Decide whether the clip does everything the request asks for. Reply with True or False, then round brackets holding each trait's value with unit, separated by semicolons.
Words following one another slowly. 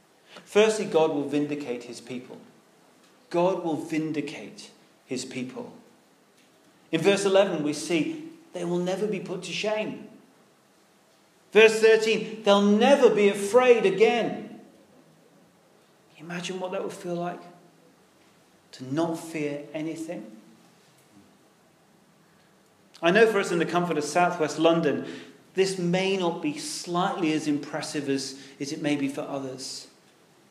True (130 wpm)